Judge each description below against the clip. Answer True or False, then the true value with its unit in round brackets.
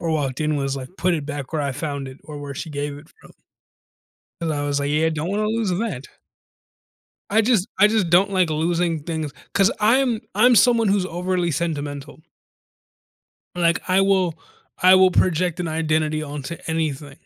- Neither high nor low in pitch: True (165 Hz)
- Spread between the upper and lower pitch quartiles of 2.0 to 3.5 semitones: False (4.2 semitones)